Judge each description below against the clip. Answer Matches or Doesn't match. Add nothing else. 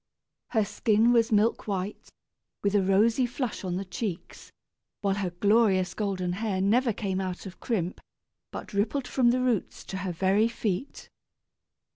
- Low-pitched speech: Doesn't match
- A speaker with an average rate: Matches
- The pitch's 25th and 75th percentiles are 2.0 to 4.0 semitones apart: Matches